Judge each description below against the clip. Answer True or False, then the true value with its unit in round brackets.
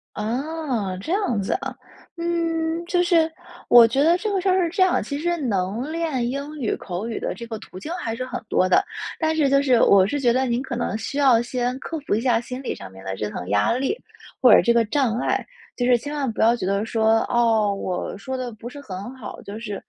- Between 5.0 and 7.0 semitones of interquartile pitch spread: True (5.4 semitones)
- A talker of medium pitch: False (245 Hz)